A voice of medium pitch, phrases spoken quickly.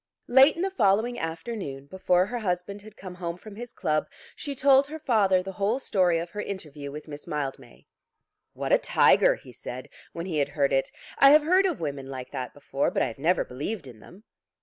Yes: medium, 180 Hz; fast, 215 wpm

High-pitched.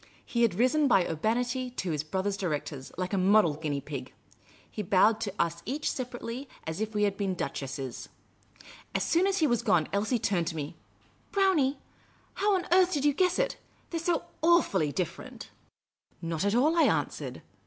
Yes: high, 215 Hz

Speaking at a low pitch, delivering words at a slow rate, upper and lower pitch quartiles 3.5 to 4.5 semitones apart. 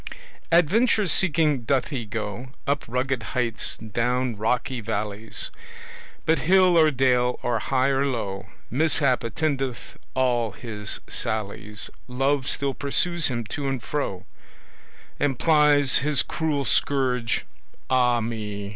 Yes: low, 130 Hz; slow, 120 wpm; average, 3.9 semitones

